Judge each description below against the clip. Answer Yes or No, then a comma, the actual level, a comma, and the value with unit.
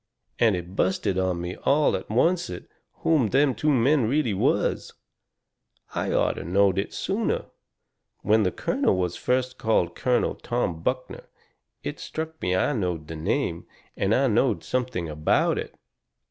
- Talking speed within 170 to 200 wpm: No, average, 145 wpm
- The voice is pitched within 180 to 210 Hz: No, low, 110 Hz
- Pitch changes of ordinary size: No, wide, 6.3 semitones